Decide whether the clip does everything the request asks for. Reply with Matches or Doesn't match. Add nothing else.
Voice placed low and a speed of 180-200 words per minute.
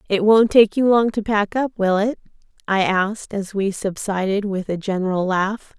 Doesn't match